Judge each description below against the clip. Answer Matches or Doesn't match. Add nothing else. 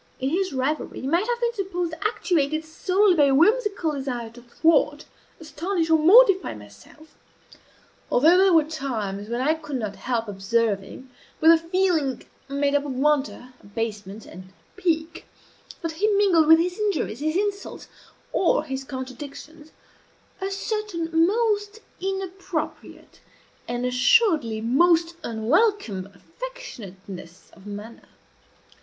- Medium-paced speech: Doesn't match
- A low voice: Doesn't match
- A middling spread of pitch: Doesn't match